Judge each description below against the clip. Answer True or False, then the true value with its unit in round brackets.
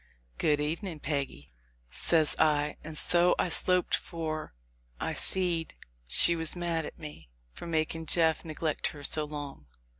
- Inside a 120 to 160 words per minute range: True (150 wpm)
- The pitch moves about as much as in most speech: False (2.1 semitones)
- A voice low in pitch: False (155 Hz)